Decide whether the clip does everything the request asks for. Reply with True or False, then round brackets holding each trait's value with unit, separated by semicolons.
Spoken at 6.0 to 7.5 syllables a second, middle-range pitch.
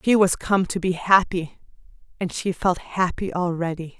False (4.6 syllables/s; 180 Hz)